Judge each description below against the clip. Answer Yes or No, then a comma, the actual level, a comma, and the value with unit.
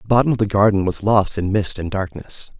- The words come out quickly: Yes, fast, 255 wpm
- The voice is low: Yes, low, 100 Hz